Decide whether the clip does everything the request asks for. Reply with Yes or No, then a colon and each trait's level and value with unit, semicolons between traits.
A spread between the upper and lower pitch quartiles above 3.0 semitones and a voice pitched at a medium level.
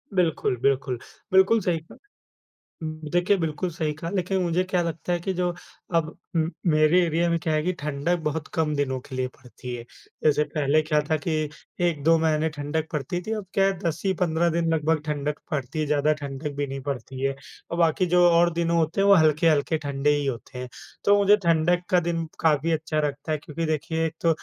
No: narrow, 2.6 semitones; medium, 160 Hz